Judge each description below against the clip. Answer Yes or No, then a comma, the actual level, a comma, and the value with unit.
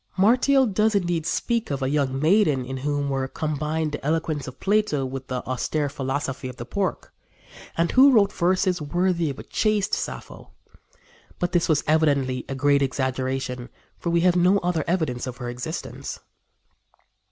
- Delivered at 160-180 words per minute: Yes, average, 165 wpm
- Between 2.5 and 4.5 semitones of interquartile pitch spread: No, average, 5.2 semitones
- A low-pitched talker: No, medium, 150 Hz